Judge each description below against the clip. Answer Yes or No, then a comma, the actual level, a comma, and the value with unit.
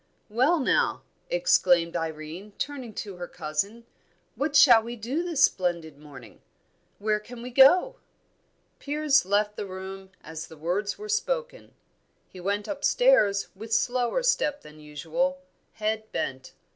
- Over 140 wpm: No, slow, 135 wpm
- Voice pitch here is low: No, high, 215 Hz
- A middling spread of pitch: No, wide, 8.1 semitones